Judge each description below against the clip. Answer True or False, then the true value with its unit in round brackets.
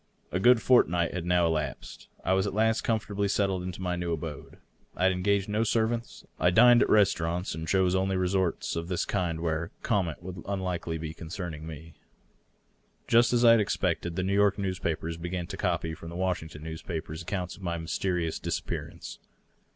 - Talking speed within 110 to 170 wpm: False (185 wpm)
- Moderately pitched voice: False (90 Hz)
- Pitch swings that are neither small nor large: True (3.2 semitones)